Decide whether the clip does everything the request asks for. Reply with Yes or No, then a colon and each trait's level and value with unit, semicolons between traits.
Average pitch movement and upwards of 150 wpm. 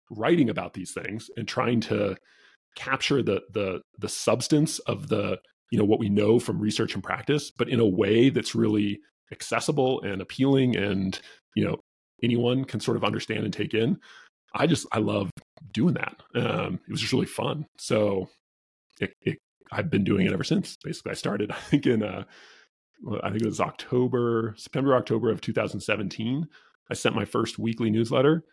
Yes: average, 3.0 semitones; average, 180 wpm